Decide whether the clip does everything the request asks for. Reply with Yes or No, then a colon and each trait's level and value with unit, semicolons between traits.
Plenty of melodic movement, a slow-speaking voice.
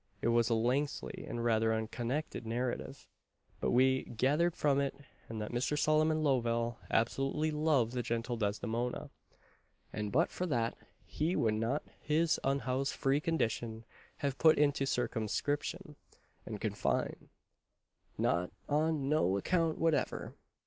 No: average, 4.5 semitones; slow, 130 wpm